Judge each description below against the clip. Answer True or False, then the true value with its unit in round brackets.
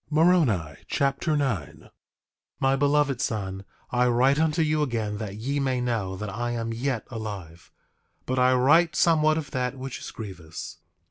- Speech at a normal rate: True (160 wpm)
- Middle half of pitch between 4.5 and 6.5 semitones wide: True (5.1 semitones)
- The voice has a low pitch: True (125 Hz)